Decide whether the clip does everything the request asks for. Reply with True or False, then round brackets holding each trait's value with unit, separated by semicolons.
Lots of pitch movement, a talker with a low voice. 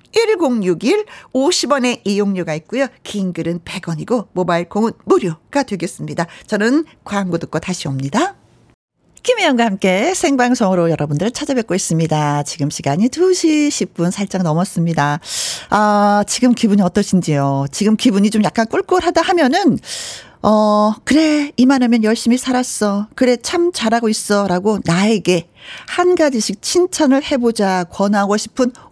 False (6.8 semitones; 215 Hz)